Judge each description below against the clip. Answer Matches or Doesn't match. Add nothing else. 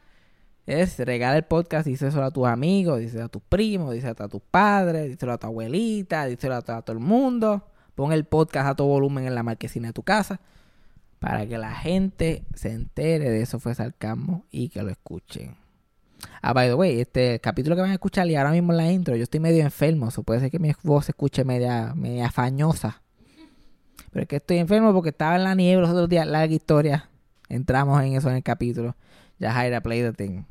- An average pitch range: Doesn't match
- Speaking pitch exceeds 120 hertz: Matches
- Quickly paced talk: Matches